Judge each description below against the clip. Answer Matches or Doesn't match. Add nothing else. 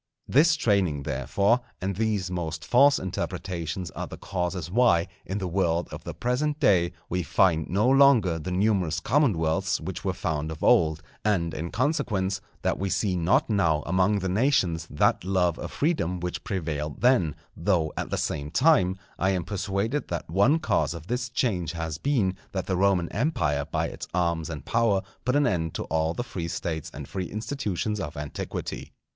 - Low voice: Matches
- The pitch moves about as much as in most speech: Matches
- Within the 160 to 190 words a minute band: Matches